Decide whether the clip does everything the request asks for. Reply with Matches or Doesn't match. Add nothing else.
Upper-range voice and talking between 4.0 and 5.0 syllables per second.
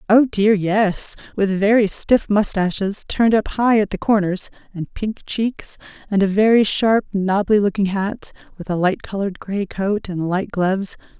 Matches